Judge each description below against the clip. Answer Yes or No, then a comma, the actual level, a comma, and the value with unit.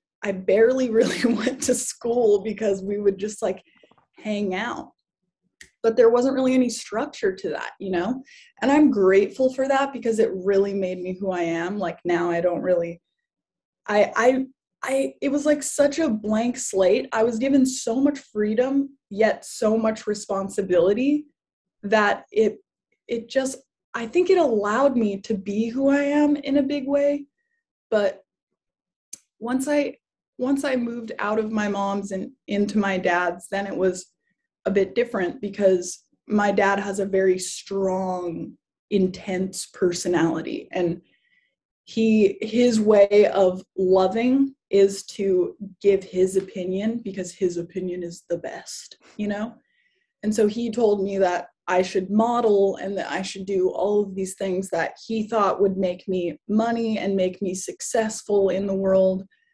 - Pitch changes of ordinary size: Yes, average, 4.6 semitones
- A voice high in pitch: Yes, high, 205 Hz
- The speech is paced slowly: No, average, 160 wpm